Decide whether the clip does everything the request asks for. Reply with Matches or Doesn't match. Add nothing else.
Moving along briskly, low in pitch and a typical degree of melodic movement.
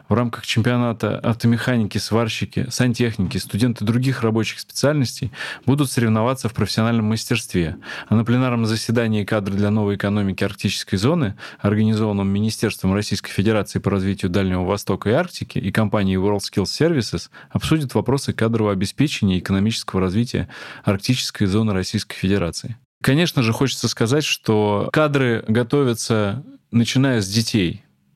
Doesn't match